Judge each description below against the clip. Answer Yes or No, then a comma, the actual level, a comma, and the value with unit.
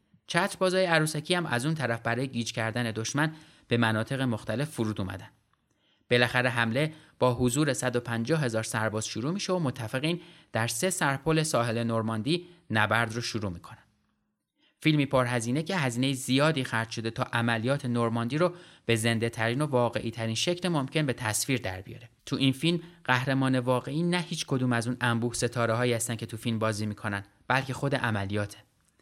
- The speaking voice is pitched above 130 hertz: No, low, 125 Hz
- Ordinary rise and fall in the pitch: Yes, average, 4.8 semitones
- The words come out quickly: Yes, fast, 165 wpm